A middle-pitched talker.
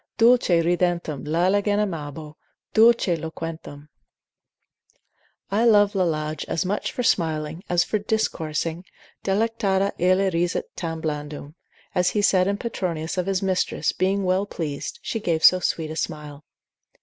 Yes: medium, 180 Hz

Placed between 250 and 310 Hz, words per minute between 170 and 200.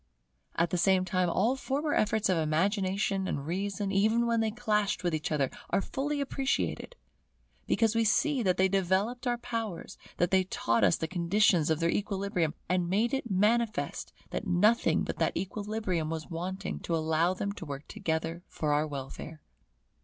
No: high, 190 Hz; average, 175 wpm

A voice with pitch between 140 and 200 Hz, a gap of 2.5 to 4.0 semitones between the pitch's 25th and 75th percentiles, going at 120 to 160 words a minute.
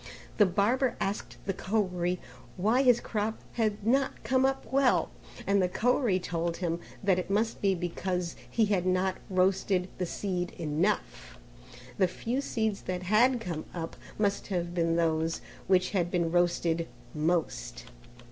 Yes: medium, 185 Hz; average, 3.6 semitones; average, 150 wpm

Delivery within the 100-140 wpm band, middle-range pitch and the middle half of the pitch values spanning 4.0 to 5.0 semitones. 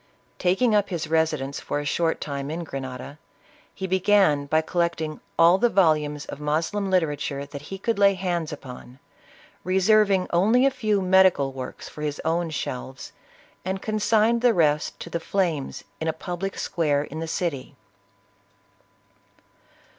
No: average, 150 wpm; medium, 165 Hz; average, 4.6 semitones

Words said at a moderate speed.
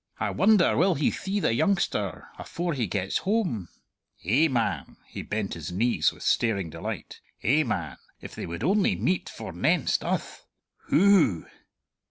Yes: average, 150 wpm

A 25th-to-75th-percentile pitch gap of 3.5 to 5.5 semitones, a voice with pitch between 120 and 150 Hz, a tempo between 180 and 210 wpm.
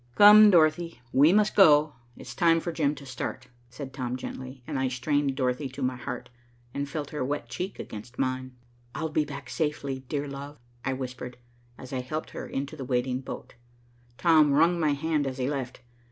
No: average, 3.1 semitones; medium, 140 Hz; average, 190 wpm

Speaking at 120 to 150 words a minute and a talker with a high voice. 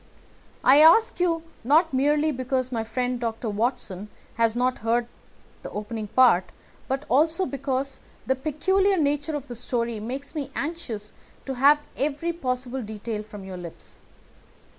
Yes: average, 145 wpm; very high, 260 Hz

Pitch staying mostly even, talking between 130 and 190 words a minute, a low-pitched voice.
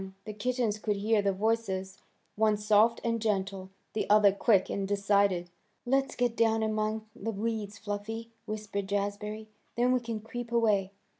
No: narrow, 2.0 semitones; average, 155 wpm; high, 215 Hz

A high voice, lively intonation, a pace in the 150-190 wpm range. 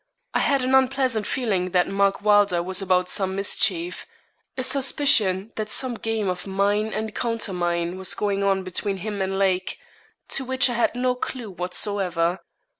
No: high, 200 Hz; average, 3.6 semitones; average, 165 wpm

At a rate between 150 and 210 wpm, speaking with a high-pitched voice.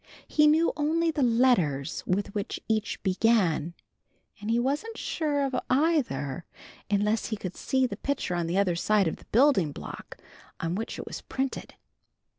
Yes: average, 165 wpm; high, 220 Hz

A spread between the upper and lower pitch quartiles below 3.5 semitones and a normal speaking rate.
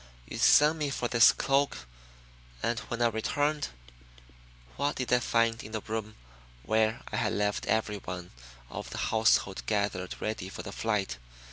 Yes: average, 3.1 semitones; average, 155 wpm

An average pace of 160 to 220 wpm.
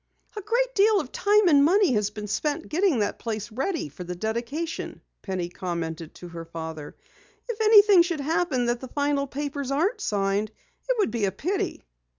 Yes: average, 180 wpm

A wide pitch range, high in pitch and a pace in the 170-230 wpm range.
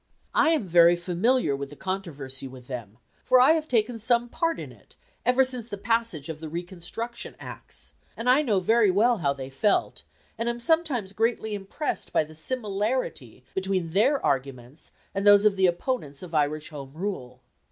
Yes: wide, 7.6 semitones; high, 195 Hz; average, 180 wpm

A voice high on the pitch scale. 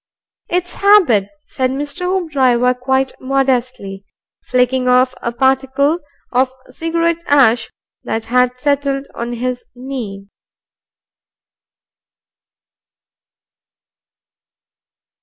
Yes: very high, 260 Hz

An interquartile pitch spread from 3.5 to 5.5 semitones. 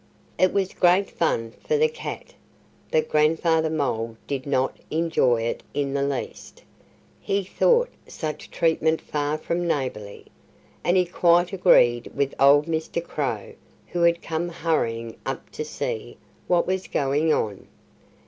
Yes: average, 4.3 semitones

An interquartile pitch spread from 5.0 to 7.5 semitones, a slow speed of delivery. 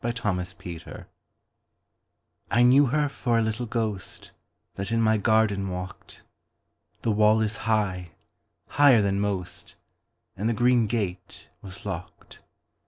No: average, 3.2 semitones; slow, 110 wpm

